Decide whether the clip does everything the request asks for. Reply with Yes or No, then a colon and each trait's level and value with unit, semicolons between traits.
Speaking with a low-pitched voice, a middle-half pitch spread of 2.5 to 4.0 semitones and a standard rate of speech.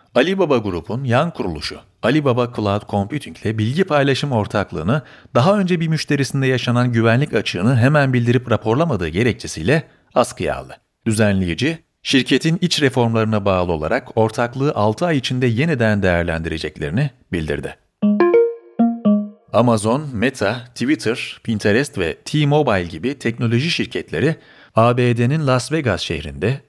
No: low, 120 Hz; average, 5.3 semitones; average, 110 wpm